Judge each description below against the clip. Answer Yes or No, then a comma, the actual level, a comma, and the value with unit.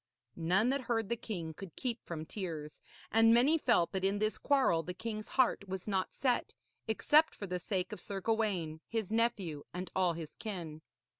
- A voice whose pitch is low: No, high, 200 Hz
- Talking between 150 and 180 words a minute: No, average, 190 wpm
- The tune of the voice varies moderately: Yes, average, 4.6 semitones